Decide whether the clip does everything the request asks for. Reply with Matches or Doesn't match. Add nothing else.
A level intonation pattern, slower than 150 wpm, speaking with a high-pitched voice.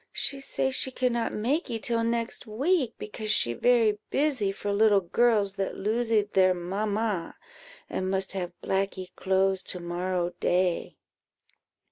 Doesn't match